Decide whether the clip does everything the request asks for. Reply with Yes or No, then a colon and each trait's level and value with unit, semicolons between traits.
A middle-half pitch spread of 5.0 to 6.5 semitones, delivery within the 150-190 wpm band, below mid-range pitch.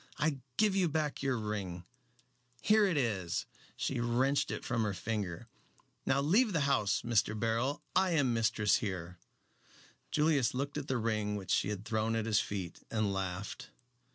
Yes: average, 5.3 semitones; average, 165 wpm; low, 115 Hz